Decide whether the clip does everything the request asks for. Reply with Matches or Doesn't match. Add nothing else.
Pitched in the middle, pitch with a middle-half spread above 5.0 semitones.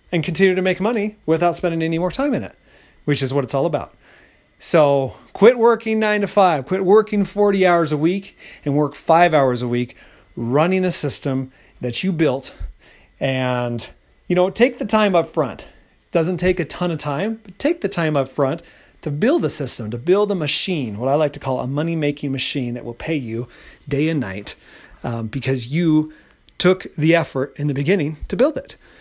Matches